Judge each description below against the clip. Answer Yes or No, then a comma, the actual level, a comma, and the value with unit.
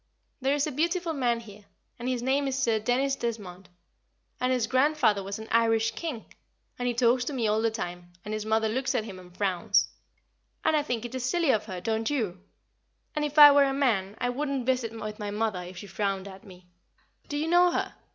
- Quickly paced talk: Yes, fast, 220 wpm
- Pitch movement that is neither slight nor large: Yes, average, 4.5 semitones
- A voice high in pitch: Yes, high, 230 Hz